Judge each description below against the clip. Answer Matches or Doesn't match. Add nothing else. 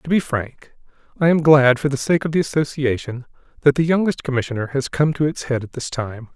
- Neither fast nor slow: Doesn't match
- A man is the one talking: Matches